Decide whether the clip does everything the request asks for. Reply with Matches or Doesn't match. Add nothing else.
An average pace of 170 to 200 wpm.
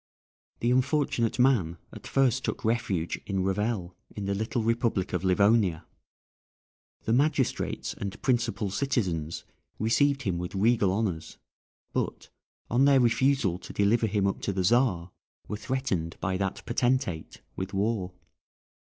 Doesn't match